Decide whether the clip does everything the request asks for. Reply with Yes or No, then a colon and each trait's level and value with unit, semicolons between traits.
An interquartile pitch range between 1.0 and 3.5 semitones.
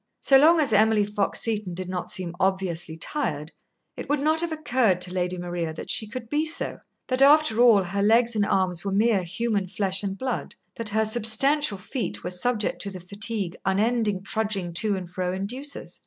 No: average, 4.5 semitones